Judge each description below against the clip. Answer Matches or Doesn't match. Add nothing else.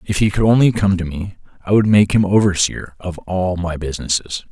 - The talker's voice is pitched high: Doesn't match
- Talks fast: Matches